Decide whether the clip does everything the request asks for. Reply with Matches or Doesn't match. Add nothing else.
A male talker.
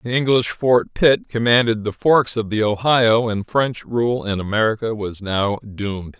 Matches